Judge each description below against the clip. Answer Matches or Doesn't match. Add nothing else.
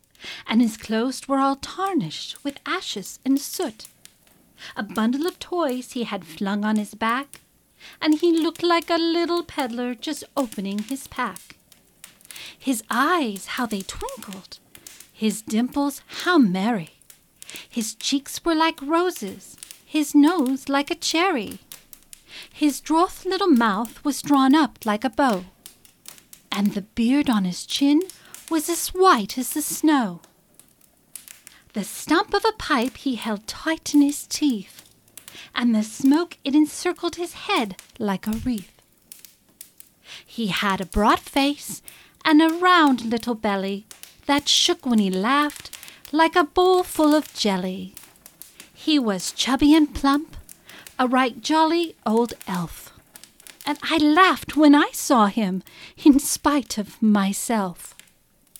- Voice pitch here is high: Matches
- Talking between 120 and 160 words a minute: Matches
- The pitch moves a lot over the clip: Matches